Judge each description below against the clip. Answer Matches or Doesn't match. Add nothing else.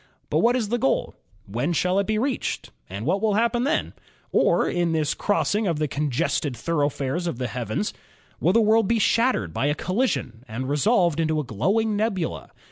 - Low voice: Doesn't match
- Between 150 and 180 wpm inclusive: Doesn't match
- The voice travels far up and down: Matches